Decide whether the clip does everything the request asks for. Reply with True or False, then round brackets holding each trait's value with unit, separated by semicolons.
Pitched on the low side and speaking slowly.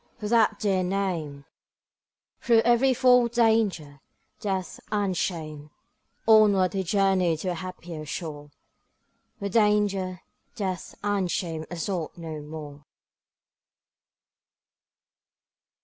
False (185 Hz; 100 wpm)